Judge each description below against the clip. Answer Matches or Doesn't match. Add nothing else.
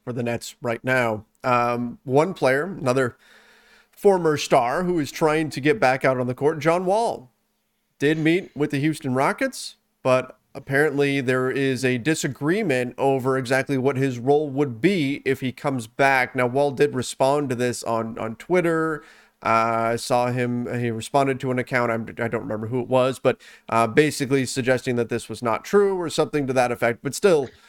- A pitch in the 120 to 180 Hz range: Matches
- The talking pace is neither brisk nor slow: Matches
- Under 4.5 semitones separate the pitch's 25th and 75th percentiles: Matches